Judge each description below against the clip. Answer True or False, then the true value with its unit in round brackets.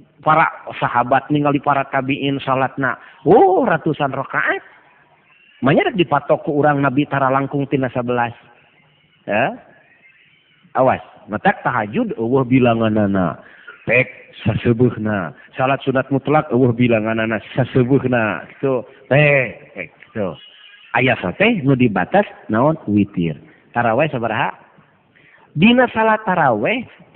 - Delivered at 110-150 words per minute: True (135 wpm)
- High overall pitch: False (135 Hz)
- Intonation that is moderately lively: True (3.6 semitones)